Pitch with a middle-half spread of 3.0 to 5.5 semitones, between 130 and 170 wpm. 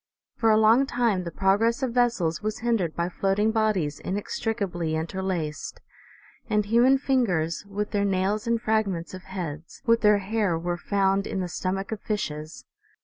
Yes: average, 3.9 semitones; average, 160 wpm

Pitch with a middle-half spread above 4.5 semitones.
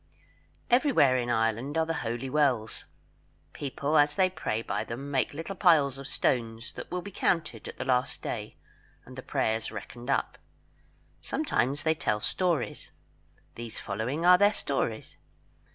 Yes: wide, 5.6 semitones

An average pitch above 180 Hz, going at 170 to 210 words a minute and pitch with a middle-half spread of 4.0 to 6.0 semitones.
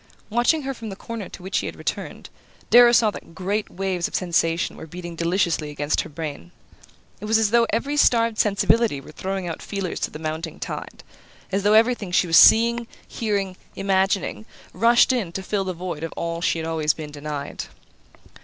Yes: high, 190 Hz; average, 190 wpm; average, 5.1 semitones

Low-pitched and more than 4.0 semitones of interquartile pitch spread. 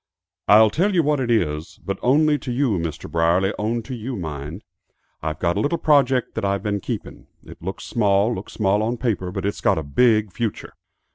Yes: low, 105 Hz; average, 5.3 semitones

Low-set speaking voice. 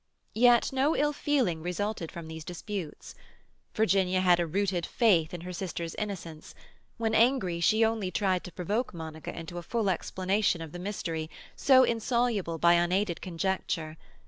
No: medium, 185 Hz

